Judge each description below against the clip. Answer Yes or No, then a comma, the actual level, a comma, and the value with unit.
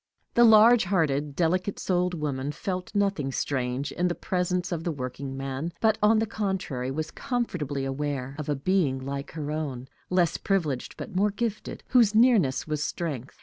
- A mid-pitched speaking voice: Yes, medium, 165 Hz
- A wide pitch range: Yes, wide, 5.9 semitones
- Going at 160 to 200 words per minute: Yes, average, 165 wpm